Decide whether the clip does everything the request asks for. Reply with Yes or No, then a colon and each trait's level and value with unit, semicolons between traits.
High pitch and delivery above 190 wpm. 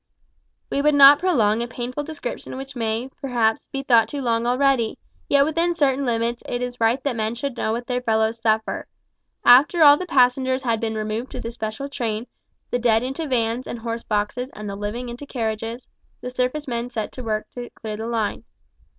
Yes: high, 245 Hz; average, 200 wpm